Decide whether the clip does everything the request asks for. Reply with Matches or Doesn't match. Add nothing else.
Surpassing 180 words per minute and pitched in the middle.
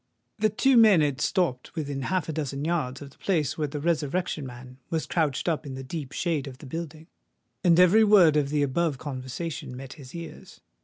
Matches